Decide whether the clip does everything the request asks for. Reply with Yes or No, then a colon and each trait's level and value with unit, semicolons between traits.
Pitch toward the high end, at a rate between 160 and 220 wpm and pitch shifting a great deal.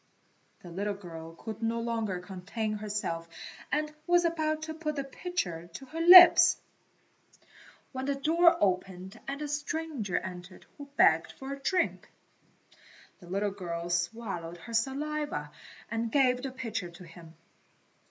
No: high, 225 Hz; average, 145 wpm; wide, 8.3 semitones